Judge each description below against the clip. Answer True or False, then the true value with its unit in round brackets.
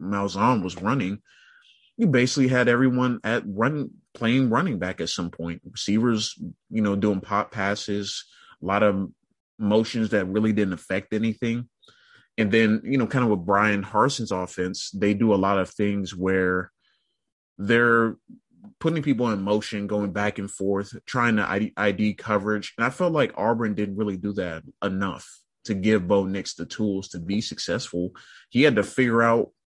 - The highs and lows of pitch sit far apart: False (2.8 semitones)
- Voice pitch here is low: True (105 Hz)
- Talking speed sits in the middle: True (170 wpm)